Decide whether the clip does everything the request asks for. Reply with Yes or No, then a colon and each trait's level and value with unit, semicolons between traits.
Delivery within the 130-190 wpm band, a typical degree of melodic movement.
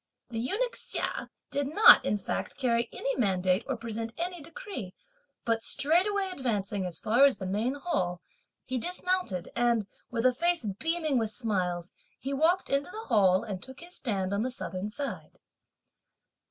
No: average, 165 wpm; wide, 7.8 semitones